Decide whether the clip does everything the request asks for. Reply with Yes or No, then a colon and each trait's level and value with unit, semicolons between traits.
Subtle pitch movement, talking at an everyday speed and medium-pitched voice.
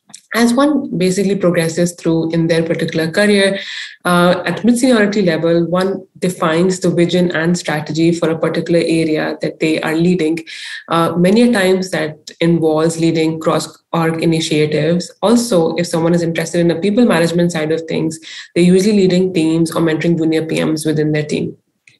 Yes: narrow, 2.2 semitones; average, 165 wpm; medium, 170 Hz